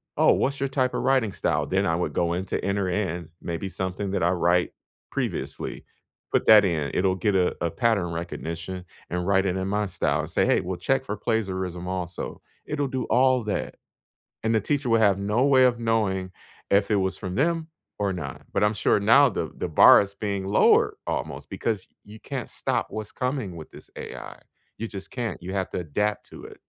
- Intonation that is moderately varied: Yes, average, 3.7 semitones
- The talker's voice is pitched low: Yes, low, 100 Hz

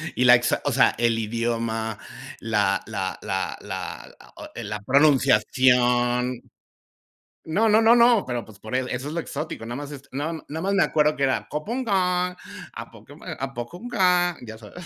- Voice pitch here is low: Yes, low, 130 Hz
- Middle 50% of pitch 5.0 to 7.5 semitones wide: Yes, wide, 5.6 semitones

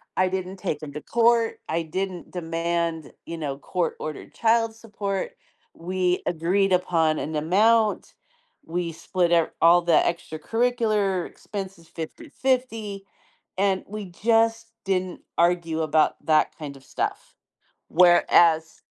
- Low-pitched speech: No, medium, 180 Hz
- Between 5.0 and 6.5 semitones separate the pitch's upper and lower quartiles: No, average, 3.9 semitones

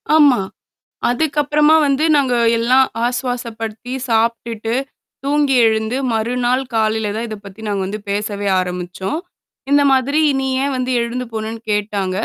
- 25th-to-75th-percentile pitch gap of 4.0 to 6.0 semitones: No, average, 3.5 semitones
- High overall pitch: Yes, high, 235 Hz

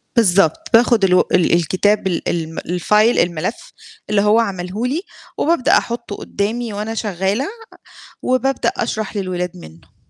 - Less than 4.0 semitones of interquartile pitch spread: No, average, 4.5 semitones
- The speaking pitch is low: No, high, 205 Hz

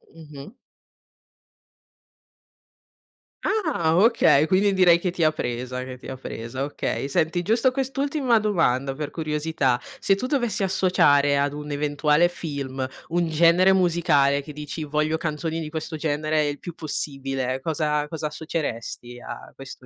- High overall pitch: No, medium, 155 Hz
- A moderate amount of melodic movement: Yes, average, 3.7 semitones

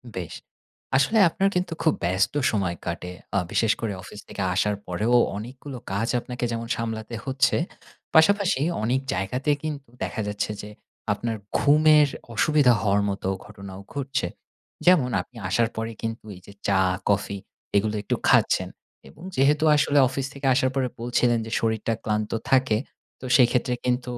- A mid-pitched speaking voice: No, low, 120 Hz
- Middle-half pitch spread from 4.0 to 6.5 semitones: Yes, average, 4.6 semitones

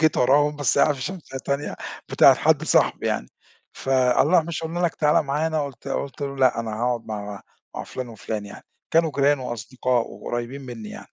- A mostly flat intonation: No, average, 3.8 semitones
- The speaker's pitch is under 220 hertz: Yes, low, 135 Hz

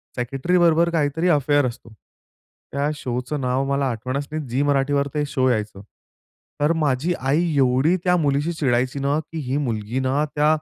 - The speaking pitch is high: No, medium, 140 Hz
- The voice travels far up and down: No, average, 2.9 semitones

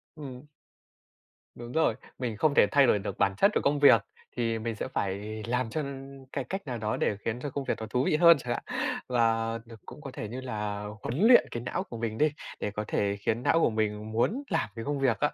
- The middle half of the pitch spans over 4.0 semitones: Yes, average, 4.4 semitones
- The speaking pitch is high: No, low, 120 Hz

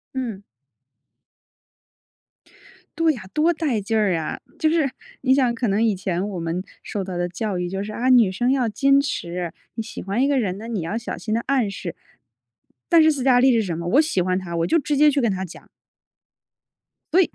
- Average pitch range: No, wide, 6.3 semitones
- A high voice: Yes, high, 225 Hz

